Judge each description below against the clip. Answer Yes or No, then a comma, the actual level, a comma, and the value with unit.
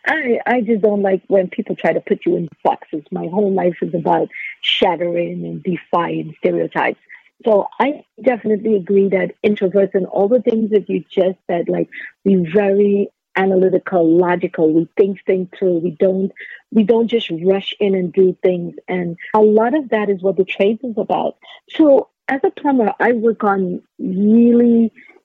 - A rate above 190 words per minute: No, average, 175 wpm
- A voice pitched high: Yes, high, 195 Hz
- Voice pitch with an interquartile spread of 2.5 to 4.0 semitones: Yes, average, 3.5 semitones